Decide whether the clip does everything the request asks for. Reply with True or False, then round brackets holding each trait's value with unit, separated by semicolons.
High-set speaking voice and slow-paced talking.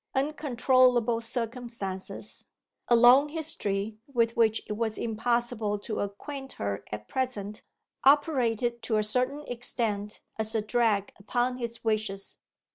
True (230 Hz; 120 wpm)